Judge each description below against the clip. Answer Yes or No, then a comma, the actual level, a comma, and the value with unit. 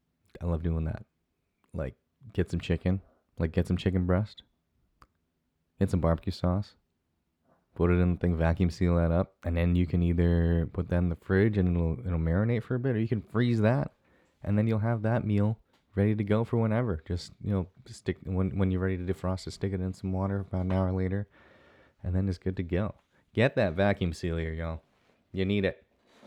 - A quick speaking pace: Yes, fast, 215 wpm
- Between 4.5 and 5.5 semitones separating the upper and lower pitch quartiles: No, average, 2.9 semitones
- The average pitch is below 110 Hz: Yes, very low, 95 Hz